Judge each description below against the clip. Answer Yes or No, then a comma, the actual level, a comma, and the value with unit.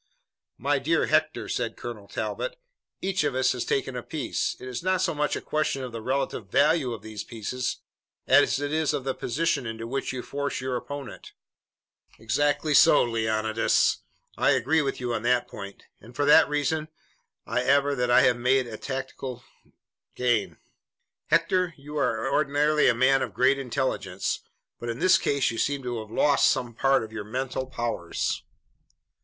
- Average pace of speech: Yes, average, 175 wpm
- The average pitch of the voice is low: Yes, low, 130 Hz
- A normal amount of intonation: Yes, average, 3.3 semitones